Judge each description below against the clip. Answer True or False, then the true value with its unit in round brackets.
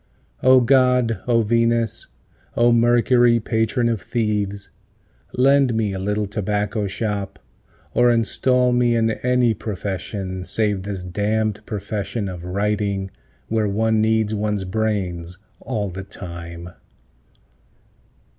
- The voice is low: True (105 Hz)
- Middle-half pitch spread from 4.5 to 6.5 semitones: False (2.9 semitones)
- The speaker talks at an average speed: False (115 wpm)